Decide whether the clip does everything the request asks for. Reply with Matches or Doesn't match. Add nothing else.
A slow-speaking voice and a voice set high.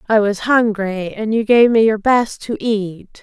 Doesn't match